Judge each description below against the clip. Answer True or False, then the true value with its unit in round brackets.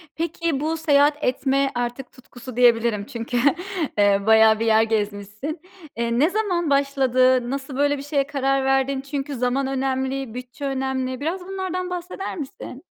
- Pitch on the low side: False (270 Hz)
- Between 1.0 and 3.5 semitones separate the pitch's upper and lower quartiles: True (2.8 semitones)